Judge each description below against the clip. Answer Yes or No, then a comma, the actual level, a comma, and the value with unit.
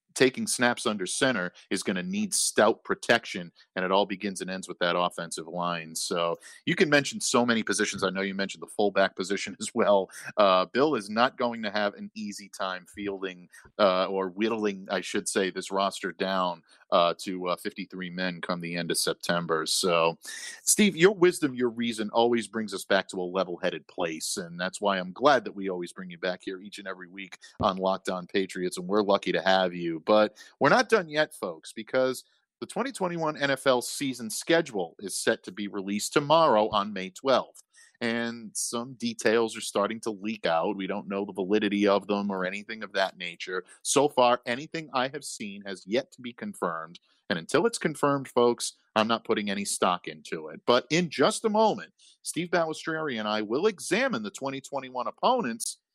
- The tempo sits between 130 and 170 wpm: No, average, 195 wpm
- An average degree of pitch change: No, wide, 6.7 semitones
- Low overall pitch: Yes, low, 105 Hz